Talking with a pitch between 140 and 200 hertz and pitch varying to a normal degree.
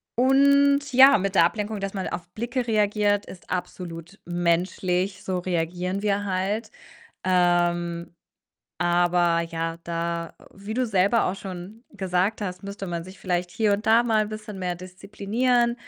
Yes: high, 190 Hz; average, 3.5 semitones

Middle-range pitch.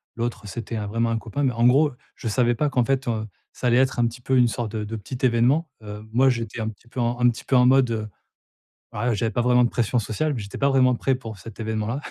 No: low, 120 Hz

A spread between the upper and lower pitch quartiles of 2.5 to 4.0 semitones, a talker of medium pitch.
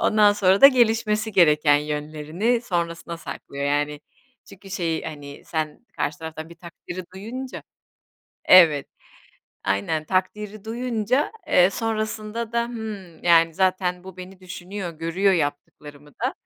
No: average, 5.2 semitones; medium, 180 Hz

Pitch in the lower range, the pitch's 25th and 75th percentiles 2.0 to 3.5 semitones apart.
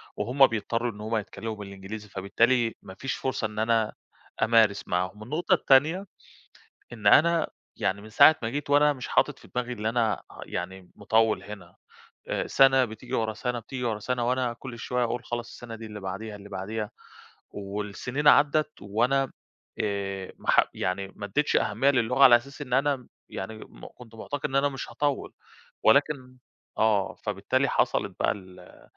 No: low, 115 Hz; average, 4.1 semitones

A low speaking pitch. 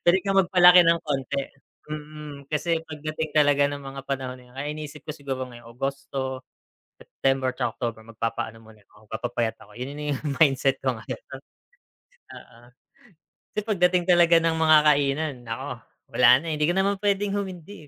No: medium, 145 Hz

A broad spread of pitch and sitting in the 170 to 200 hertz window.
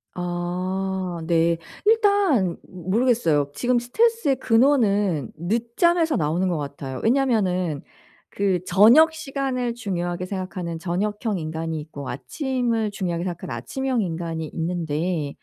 Yes: wide, 6.3 semitones; medium, 185 Hz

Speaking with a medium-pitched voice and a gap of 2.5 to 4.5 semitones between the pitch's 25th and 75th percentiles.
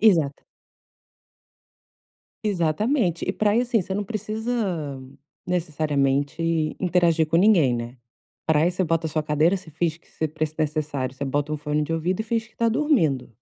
No: medium, 165 Hz; average, 4.9 semitones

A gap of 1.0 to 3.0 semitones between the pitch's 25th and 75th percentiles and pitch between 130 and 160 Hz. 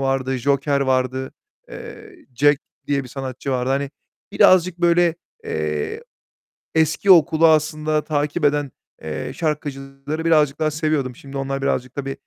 Yes: narrow, 2.6 semitones; medium, 140 Hz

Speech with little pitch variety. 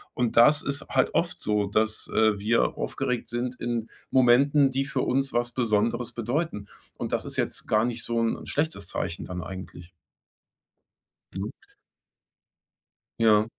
No: average, 3.1 semitones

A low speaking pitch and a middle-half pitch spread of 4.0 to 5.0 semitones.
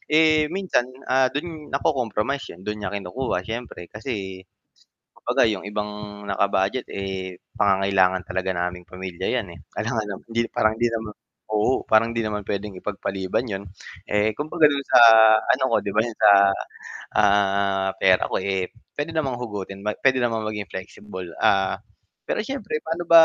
Yes: low, 105 Hz; average, 4.7 semitones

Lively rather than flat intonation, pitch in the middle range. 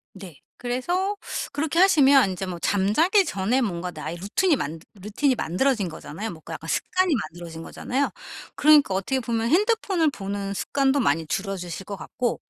No: wide, 7.6 semitones; high, 225 Hz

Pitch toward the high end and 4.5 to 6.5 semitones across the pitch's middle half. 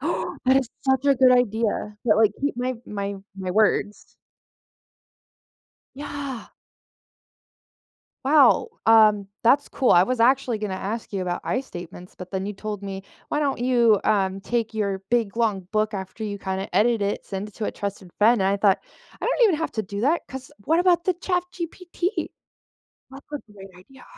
Yes: high, 220 Hz; average, 4.9 semitones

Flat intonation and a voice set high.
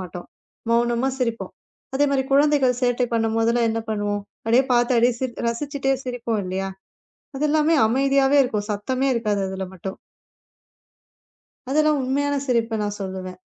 No: average, 4.3 semitones; high, 240 Hz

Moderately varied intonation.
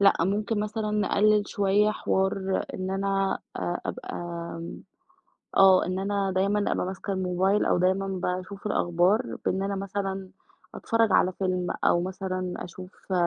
No: narrow, 1.6 semitones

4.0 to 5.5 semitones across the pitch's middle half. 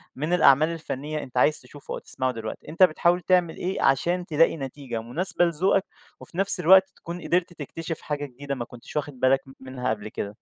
Yes: average, 4.9 semitones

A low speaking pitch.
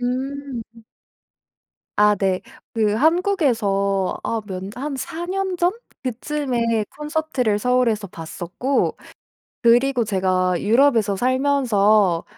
No: high, 235 Hz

